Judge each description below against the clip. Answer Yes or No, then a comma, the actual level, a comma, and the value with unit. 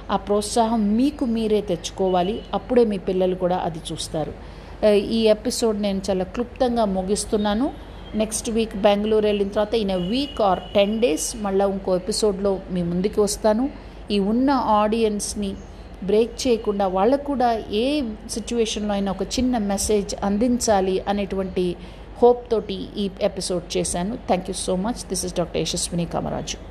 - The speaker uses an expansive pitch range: No, average, 2.9 semitones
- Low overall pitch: No, high, 210 Hz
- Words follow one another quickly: Yes, fast, 140 wpm